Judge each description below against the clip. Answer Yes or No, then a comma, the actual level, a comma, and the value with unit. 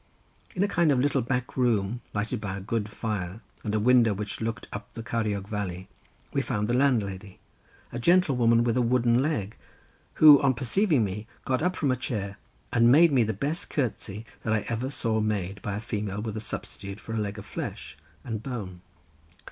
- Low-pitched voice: Yes, low, 115 Hz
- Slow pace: No, average, 200 wpm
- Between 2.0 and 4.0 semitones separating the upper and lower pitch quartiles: Yes, average, 3.5 semitones